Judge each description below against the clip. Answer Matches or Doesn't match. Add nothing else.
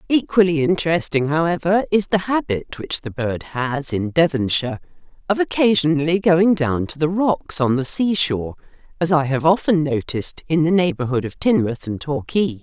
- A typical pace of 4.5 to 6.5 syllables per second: Matches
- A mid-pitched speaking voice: Matches